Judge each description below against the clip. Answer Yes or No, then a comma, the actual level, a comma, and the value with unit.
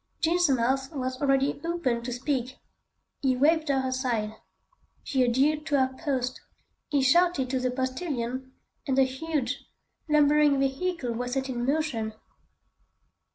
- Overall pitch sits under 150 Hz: No, very high, 265 Hz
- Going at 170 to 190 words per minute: No, slow, 135 wpm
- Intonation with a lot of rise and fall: No, narrow, 2.6 semitones